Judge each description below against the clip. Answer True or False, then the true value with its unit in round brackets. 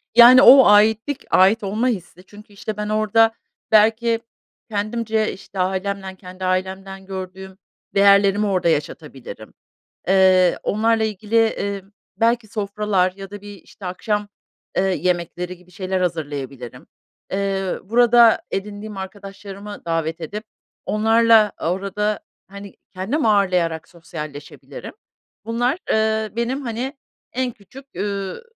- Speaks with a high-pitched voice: True (200 Hz)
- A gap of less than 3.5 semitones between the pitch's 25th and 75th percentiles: True (2.8 semitones)